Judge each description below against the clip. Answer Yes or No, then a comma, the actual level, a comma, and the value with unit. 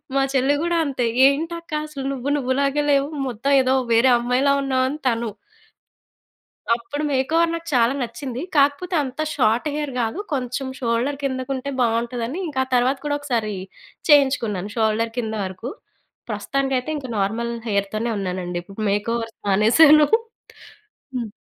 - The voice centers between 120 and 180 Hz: No, very high, 255 Hz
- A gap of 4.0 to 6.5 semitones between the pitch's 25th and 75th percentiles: No, average, 3.5 semitones